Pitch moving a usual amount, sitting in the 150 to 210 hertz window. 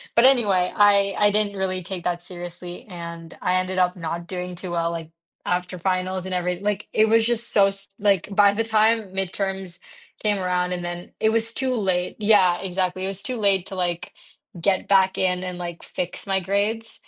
No: narrow, 2.3 semitones; high, 190 Hz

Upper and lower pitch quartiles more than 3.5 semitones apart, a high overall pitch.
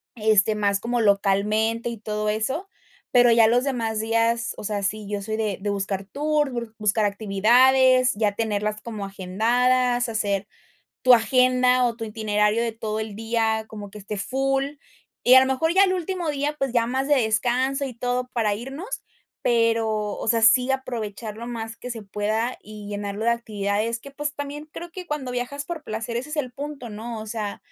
No: average, 3.2 semitones; high, 230 Hz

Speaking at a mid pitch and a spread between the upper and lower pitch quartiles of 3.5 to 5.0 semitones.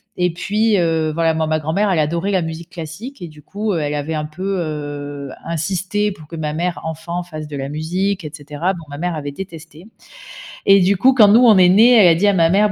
Yes: medium, 170 Hz; average, 3.8 semitones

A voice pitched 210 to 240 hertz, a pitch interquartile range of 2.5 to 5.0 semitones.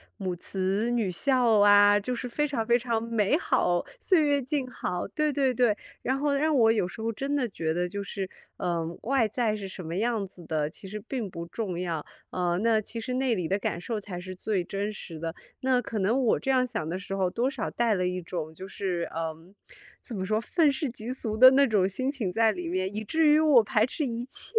No: high, 215 Hz; wide, 5.5 semitones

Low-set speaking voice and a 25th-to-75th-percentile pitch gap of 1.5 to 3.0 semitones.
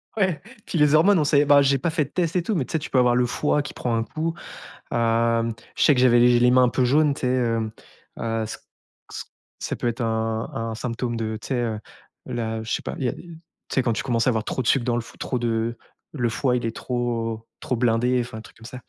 No: low, 120 Hz; average, 3.4 semitones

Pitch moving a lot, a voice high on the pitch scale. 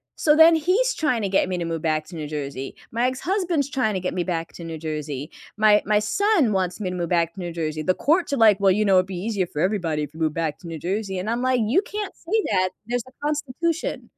Yes: wide, 7.9 semitones; high, 195 Hz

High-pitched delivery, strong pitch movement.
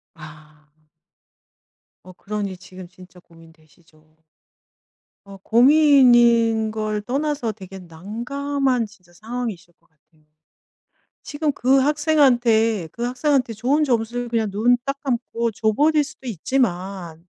Yes: high, 225 Hz; wide, 5.9 semitones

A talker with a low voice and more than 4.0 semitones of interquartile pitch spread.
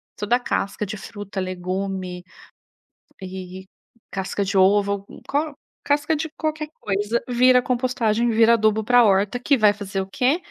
No: high, 210 Hz; average, 4.4 semitones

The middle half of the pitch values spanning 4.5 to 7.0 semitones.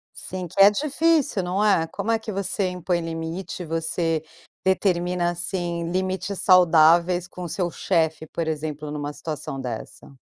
No: narrow, 2.6 semitones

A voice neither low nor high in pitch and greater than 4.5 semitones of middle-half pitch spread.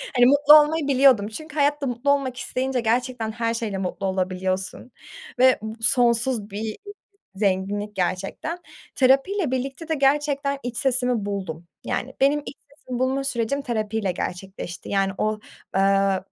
No: high, 240 Hz; average, 5.3 semitones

